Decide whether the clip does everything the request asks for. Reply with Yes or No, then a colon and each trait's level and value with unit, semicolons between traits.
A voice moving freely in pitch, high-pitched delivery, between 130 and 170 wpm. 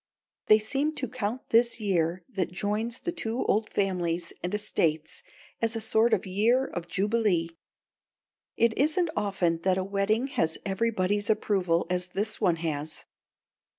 No: average, 4.2 semitones; high, 205 Hz; average, 150 wpm